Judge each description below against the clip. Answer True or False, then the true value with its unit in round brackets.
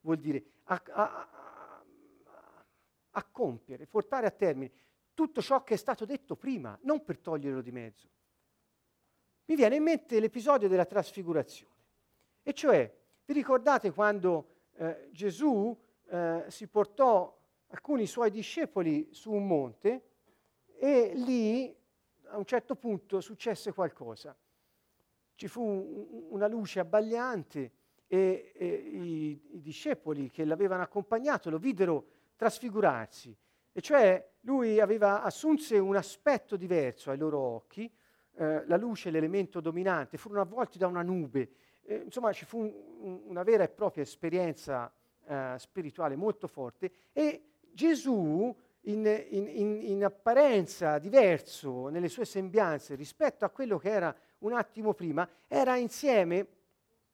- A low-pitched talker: False (200 Hz)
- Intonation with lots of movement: True (6.6 semitones)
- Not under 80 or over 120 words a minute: False (135 wpm)